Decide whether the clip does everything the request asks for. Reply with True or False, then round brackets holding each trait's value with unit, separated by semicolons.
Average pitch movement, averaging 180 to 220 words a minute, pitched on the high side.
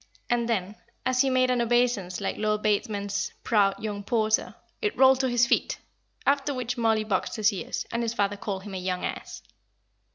True (3.3 semitones; 190 wpm; 220 Hz)